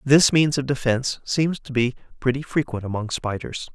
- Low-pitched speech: Yes, low, 130 Hz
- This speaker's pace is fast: No, average, 175 wpm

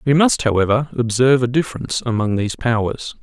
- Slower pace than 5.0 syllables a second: No, 6.3 syllables/s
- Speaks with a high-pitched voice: No, low, 125 Hz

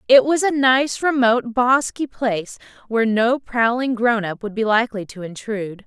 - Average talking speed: Yes, average, 175 wpm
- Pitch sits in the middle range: No, high, 235 Hz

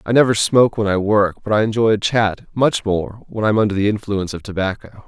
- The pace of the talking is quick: Yes, fast, 250 wpm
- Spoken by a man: Yes, male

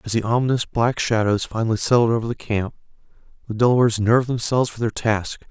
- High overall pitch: No, low, 115 Hz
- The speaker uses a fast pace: No, average, 185 wpm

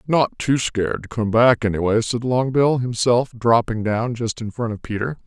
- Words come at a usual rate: Yes, average, 195 wpm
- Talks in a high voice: No, low, 115 Hz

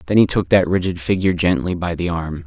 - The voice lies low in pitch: Yes, very low, 85 Hz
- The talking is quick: Yes, fast, 245 wpm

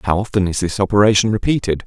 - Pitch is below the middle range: Yes, low, 100 Hz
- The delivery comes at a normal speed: Yes, average, 195 wpm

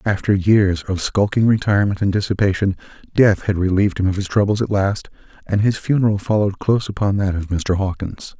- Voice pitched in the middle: No, low, 100 Hz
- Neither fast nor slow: Yes, average, 185 wpm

